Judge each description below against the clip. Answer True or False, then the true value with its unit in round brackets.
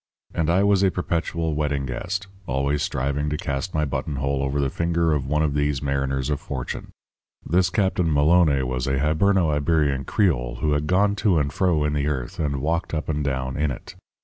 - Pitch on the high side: False (75 Hz)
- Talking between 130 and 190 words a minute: False (200 wpm)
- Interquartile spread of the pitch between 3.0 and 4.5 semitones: True (3.4 semitones)